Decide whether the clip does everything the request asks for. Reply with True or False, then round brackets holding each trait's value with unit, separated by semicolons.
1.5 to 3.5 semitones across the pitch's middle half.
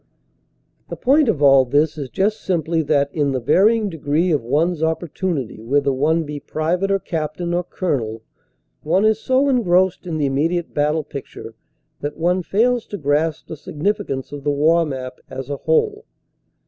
False (4.6 semitones)